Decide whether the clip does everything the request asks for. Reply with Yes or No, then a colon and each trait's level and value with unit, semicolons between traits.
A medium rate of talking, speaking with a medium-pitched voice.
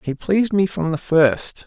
No: fast, 215 wpm; medium, 170 Hz